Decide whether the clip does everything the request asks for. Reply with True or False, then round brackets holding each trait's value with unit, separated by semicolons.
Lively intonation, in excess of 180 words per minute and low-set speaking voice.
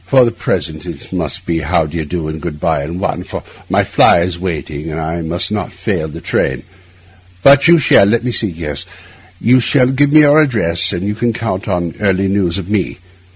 True (5.9 semitones; 200 wpm; 90 Hz)